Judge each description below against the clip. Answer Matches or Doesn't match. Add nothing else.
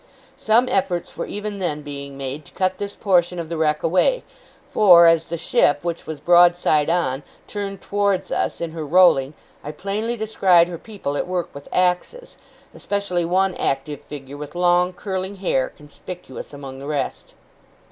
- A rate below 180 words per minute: Matches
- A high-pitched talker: Doesn't match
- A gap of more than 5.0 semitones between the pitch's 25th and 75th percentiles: Doesn't match